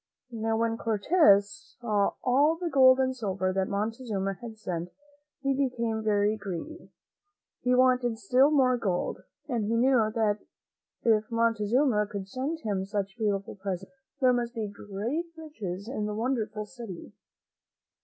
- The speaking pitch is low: No, high, 225 Hz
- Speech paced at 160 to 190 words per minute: No, average, 145 wpm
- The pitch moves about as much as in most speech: Yes, average, 3.9 semitones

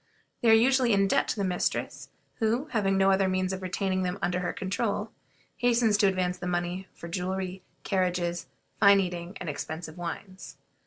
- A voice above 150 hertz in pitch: Yes, high, 190 Hz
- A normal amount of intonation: No, narrow, 1.9 semitones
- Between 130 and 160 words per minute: No, average, 175 wpm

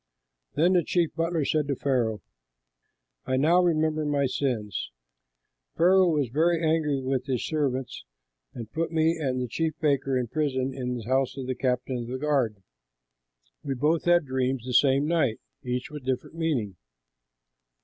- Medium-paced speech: Yes, average, 165 wpm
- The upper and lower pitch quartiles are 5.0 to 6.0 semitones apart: No, average, 3.8 semitones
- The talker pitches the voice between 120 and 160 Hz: Yes, low, 135 Hz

